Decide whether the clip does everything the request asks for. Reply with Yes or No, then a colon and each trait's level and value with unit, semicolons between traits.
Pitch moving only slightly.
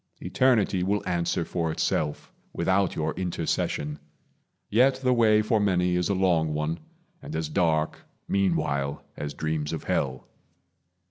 No: average, 4.1 semitones